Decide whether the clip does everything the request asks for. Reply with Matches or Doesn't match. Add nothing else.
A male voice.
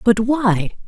Doesn't match